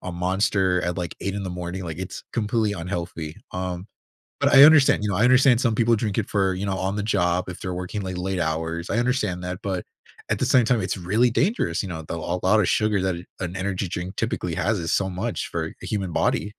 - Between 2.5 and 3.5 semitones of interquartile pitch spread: Yes, average, 3.1 semitones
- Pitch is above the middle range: No, very low, 95 Hz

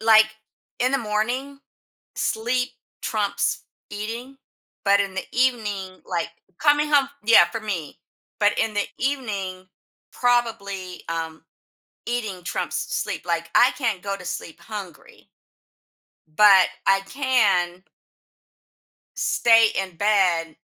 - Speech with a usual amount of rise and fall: Yes, average, 4.5 semitones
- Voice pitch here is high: Yes, high, 210 Hz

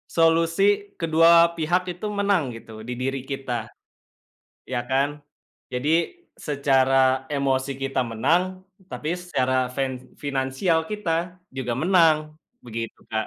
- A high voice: No, medium, 140 Hz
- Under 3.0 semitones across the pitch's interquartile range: No, average, 4.0 semitones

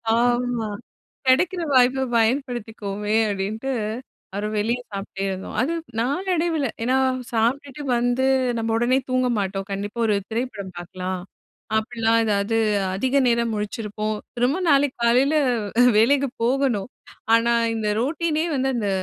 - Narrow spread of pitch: No, average, 3.8 semitones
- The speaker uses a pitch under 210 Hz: No, high, 235 Hz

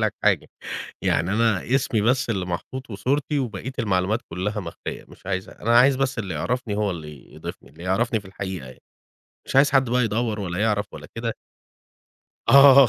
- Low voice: Yes, low, 110 Hz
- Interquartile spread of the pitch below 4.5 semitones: No, average, 5.0 semitones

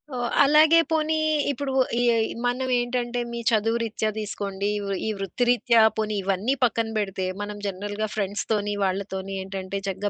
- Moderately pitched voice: No, high, 215 Hz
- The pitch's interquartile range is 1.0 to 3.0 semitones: No, average, 3.7 semitones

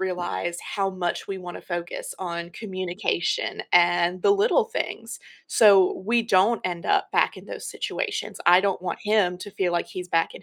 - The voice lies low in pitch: No, medium, 185 Hz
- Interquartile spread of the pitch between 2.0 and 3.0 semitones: Yes, narrow, 2.5 semitones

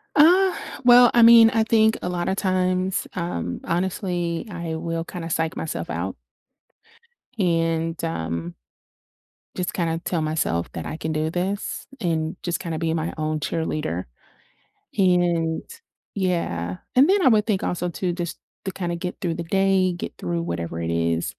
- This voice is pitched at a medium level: Yes, medium, 170 Hz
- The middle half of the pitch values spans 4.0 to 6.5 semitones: No, average, 2.9 semitones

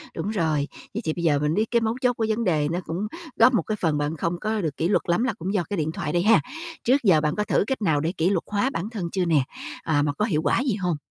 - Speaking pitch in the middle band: Yes, medium, 175 Hz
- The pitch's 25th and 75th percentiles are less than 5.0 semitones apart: No, average, 5.3 semitones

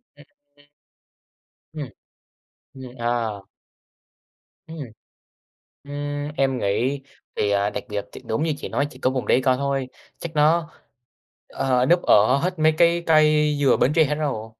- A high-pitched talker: No, medium, 145 Hz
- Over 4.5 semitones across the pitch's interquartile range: No, average, 3.2 semitones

